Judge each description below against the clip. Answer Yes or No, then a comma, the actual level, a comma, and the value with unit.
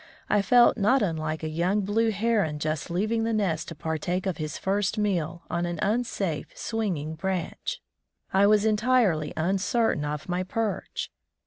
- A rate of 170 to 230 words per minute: No, average, 155 wpm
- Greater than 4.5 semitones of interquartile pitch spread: Yes, average, 5.1 semitones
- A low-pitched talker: No, high, 190 Hz